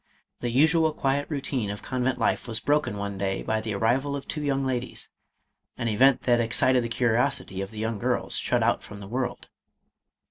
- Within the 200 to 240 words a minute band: Yes, fast, 205 wpm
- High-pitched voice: No, low, 120 Hz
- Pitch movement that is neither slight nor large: Yes, average, 3.8 semitones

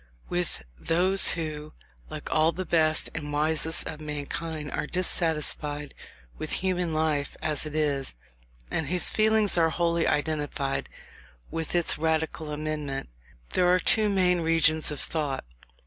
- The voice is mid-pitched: Yes, medium, 160 Hz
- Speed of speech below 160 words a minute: Yes, slow, 135 wpm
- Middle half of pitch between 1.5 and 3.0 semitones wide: Yes, narrow, 2.4 semitones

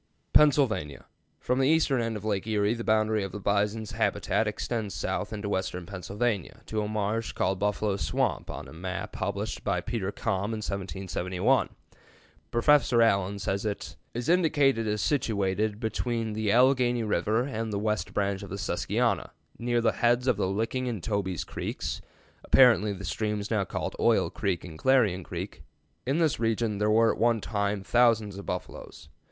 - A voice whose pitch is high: No, low, 105 Hz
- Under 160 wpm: No, average, 170 wpm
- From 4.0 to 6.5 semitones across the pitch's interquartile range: No, average, 3.0 semitones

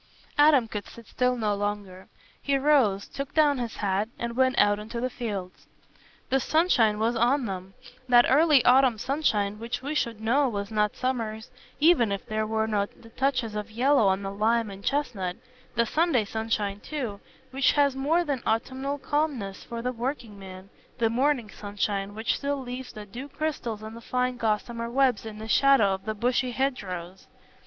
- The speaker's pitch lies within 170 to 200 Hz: No, high, 230 Hz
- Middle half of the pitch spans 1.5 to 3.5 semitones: No, average, 4.3 semitones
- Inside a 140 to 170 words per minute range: No, average, 180 wpm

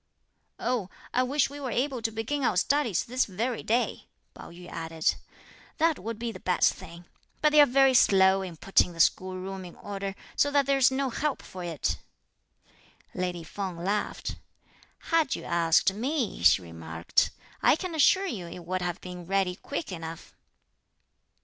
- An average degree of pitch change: No, wide, 7.1 semitones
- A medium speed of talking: Yes, average, 170 wpm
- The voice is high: Yes, high, 195 Hz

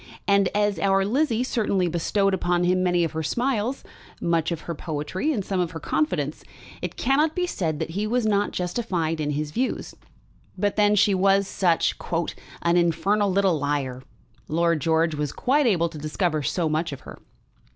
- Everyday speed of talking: Yes, average, 180 wpm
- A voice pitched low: No, medium, 180 Hz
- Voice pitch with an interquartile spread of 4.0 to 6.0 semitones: Yes, average, 4.3 semitones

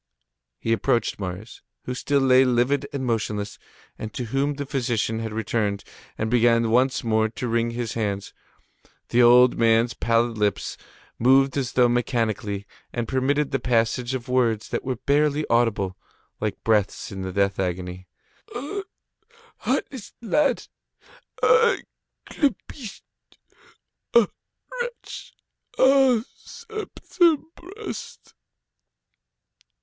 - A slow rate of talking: Yes, slow, 115 wpm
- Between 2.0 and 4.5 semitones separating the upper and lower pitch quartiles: Yes, average, 4.2 semitones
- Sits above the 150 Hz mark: No, low, 120 Hz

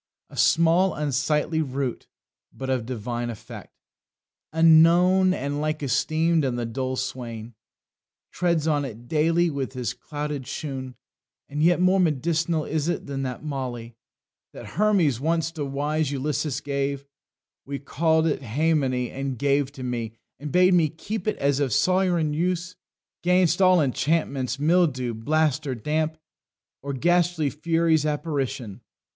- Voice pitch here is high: No, medium, 150 Hz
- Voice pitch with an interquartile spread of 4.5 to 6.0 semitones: No, average, 3.9 semitones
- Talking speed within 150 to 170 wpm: No, average, 140 wpm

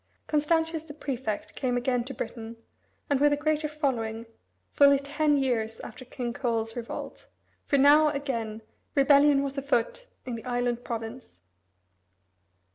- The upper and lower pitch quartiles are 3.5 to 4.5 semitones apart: Yes, average, 3.8 semitones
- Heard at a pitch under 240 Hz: No, very high, 270 Hz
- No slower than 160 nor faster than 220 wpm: No, slow, 135 wpm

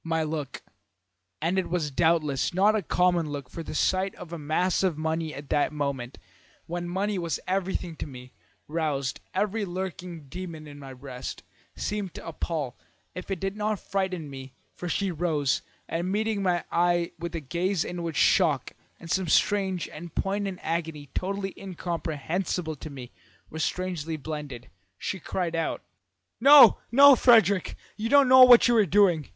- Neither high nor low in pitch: Yes, medium, 170 Hz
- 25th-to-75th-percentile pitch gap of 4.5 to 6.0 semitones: No, average, 3.9 semitones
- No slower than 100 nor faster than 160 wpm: No, average, 170 wpm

